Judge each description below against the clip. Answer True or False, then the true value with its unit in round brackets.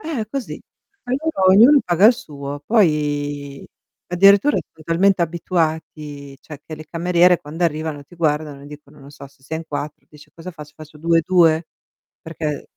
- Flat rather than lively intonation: False (3.4 semitones)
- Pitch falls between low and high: True (160 Hz)